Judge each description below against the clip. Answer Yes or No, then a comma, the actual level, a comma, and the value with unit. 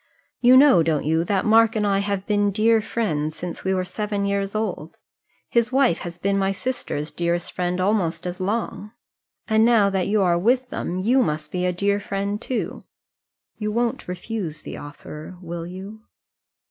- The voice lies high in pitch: Yes, high, 200 Hz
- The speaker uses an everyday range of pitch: Yes, average, 3.7 semitones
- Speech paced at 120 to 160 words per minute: No, average, 180 wpm